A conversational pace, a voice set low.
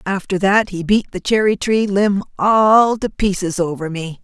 No: average, 185 wpm; high, 195 Hz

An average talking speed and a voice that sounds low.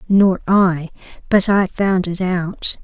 No: average, 150 wpm; medium, 185 Hz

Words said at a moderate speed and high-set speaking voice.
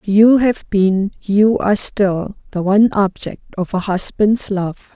Yes: average, 155 wpm; high, 200 Hz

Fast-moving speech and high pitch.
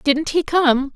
No: average, 190 wpm; very high, 295 Hz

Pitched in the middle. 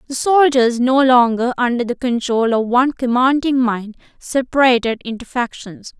No: very high, 250 Hz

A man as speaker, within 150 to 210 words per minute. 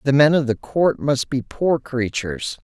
Yes: male; average, 200 wpm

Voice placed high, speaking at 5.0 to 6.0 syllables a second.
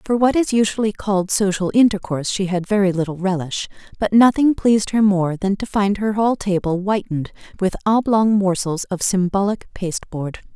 Yes: high, 200 Hz; 5.3 syllables/s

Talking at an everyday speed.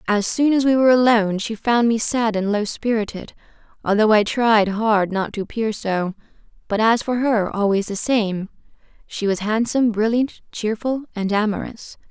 Yes: average, 175 wpm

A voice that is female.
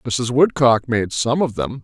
No: male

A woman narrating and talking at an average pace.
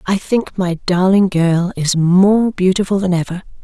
Yes: female; average, 165 wpm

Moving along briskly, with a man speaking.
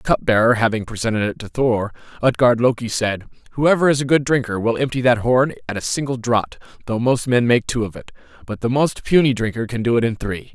Yes: fast, 230 wpm; male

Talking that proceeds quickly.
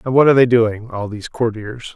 Yes: fast, 245 wpm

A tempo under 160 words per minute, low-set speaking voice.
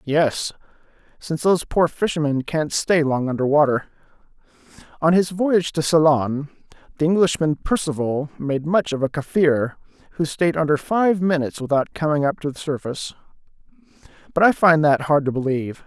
No: average, 150 wpm; medium, 155 Hz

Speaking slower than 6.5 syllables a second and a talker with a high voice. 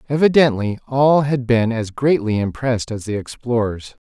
No: 4.9 syllables/s; low, 125 Hz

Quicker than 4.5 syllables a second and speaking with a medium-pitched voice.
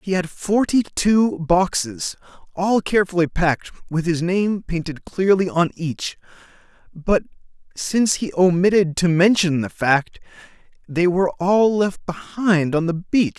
No: 4.2 syllables/s; medium, 180 Hz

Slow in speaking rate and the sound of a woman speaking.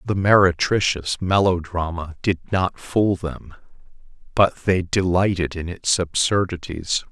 No: slow, 110 wpm; male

